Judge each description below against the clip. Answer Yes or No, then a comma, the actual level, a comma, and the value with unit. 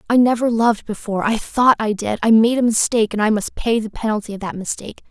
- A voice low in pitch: No, high, 220 Hz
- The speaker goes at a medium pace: No, fast, 235 wpm